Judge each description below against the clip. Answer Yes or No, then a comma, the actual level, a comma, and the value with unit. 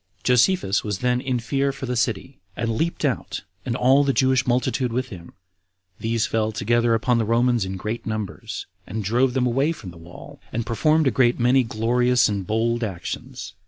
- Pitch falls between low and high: No, low, 120 Hz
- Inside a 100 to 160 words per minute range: No, average, 190 wpm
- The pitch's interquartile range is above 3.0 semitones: No, narrow, 2.6 semitones